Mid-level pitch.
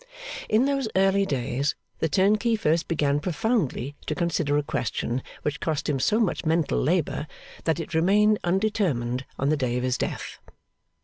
Yes: medium, 160 Hz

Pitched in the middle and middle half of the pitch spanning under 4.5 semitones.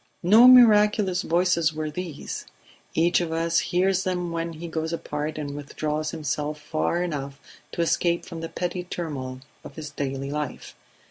Yes: medium, 165 Hz; average, 2.9 semitones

